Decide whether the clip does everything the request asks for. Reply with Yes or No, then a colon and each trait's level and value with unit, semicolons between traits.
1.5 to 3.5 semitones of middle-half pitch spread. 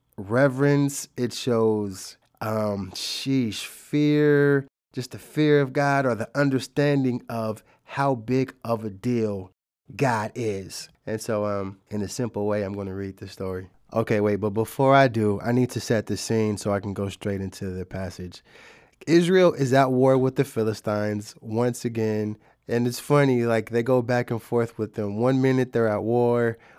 No: average, 3.9 semitones